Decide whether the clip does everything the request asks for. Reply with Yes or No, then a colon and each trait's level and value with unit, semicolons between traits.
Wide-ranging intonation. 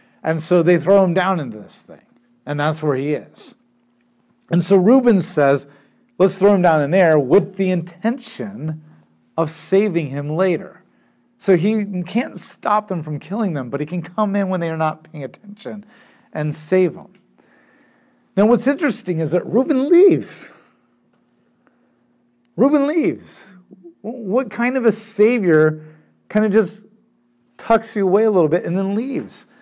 Yes: wide, 5.8 semitones